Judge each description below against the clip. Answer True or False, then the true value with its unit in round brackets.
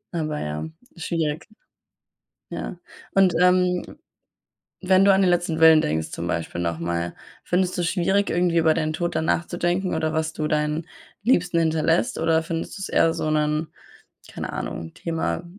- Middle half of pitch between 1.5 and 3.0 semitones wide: True (2.5 semitones)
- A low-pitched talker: False (165 Hz)